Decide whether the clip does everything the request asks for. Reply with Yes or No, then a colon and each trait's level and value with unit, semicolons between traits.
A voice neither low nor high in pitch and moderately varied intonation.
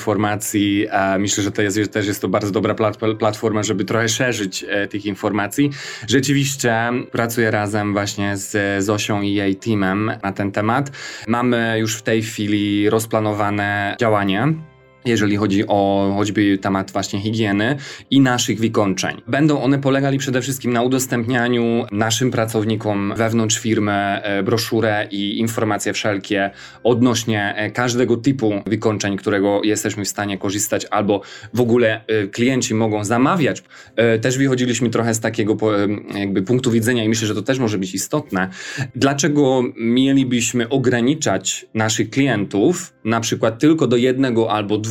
No: low, 110 Hz; average, 3.0 semitones